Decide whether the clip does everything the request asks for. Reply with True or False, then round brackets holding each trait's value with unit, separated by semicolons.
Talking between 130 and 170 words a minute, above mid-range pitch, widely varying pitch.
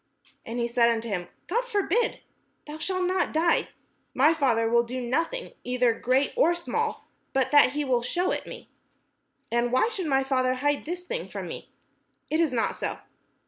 False (185 wpm; 275 Hz; 6.4 semitones)